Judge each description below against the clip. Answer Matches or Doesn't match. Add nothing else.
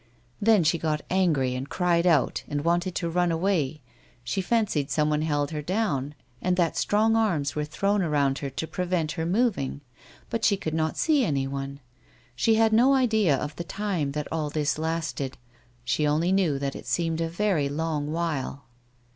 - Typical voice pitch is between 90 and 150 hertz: Doesn't match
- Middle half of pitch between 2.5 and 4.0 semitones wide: Doesn't match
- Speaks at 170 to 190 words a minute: Matches